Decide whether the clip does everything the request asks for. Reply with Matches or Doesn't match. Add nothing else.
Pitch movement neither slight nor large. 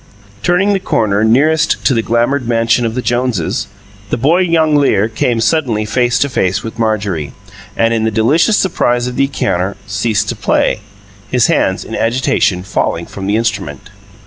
Matches